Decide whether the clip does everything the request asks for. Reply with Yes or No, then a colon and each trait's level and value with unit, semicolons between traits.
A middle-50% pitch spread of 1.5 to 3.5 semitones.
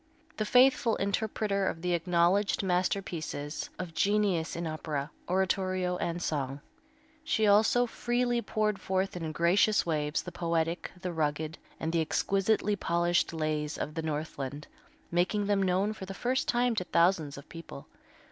No: average, 4.0 semitones